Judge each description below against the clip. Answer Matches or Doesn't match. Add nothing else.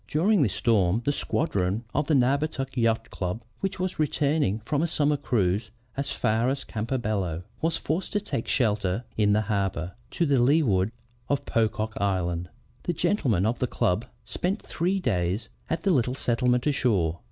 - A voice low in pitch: Matches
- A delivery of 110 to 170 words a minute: Matches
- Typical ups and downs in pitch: Doesn't match